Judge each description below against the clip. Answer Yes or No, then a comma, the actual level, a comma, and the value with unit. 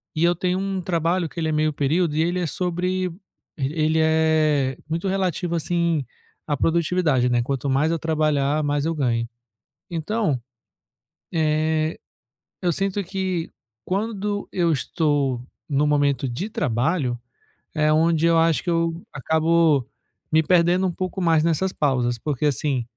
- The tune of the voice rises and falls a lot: No, average, 3.1 semitones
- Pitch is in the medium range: Yes, medium, 160 Hz